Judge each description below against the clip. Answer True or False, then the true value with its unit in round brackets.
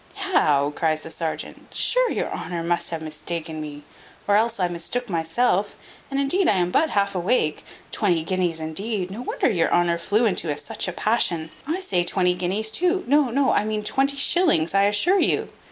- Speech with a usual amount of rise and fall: False (6.6 semitones)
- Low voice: False (190 Hz)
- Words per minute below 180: False (185 wpm)